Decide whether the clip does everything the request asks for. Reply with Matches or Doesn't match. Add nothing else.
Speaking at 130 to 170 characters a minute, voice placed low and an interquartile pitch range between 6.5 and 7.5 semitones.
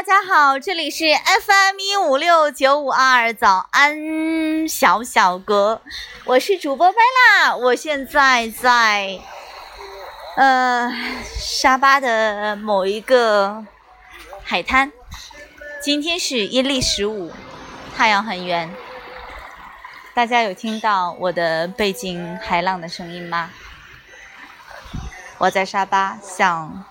Doesn't match